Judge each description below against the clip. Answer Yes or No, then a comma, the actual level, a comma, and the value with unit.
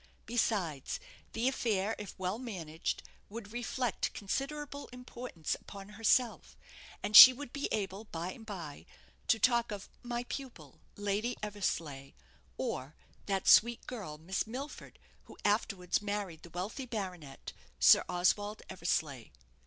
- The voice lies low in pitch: No, high, 205 Hz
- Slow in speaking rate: Yes, slow, 130 wpm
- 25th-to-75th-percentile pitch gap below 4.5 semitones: No, average, 5.0 semitones